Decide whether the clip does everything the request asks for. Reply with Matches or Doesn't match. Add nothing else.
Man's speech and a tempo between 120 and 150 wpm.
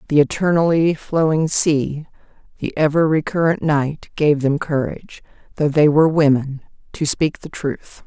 Doesn't match